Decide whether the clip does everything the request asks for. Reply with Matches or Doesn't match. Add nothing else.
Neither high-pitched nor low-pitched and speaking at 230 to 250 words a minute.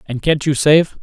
Matches